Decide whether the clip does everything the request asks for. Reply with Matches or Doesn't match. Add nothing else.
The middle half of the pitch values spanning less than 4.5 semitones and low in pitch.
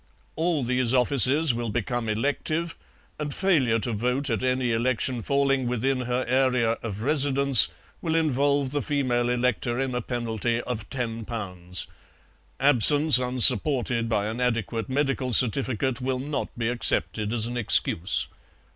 Matches